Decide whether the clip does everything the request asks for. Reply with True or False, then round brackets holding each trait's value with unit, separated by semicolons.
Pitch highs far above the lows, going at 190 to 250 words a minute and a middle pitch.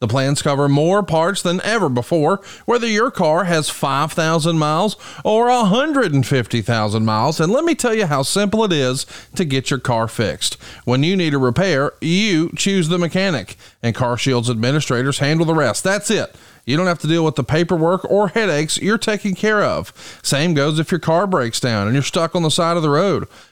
True (5.9 semitones; 200 wpm; 160 Hz)